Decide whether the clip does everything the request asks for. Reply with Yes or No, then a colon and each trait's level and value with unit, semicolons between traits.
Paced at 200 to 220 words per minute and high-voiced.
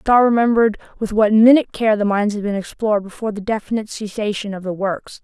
Yes: fast, 205 wpm; high, 210 Hz